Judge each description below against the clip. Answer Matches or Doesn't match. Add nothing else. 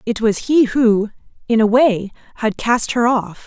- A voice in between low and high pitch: Doesn't match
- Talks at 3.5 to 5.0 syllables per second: Matches